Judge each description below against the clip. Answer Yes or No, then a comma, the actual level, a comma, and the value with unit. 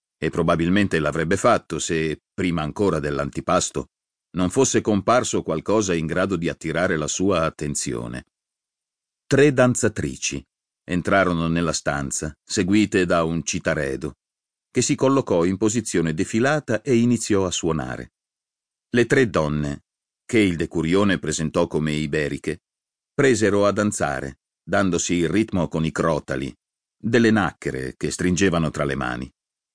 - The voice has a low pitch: Yes, very low, 85 Hz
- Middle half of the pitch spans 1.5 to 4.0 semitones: No, average, 5.2 semitones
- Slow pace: No, average, 125 wpm